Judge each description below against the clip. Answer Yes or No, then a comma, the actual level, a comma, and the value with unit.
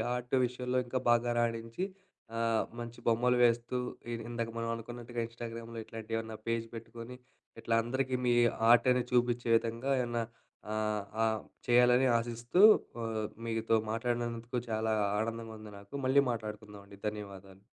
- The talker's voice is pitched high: No, low, 115 Hz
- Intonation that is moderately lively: No, narrow, 1.3 semitones